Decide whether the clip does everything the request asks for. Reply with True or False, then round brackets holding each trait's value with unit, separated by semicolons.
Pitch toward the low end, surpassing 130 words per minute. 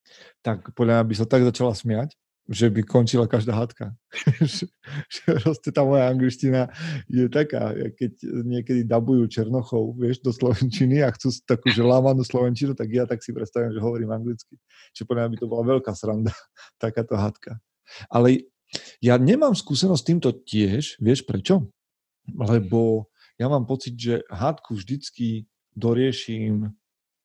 True (120 Hz; 140 wpm)